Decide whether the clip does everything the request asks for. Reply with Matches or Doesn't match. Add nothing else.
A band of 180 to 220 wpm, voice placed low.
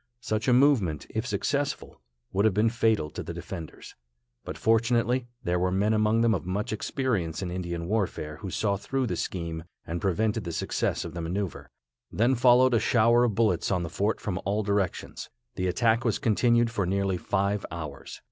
Matches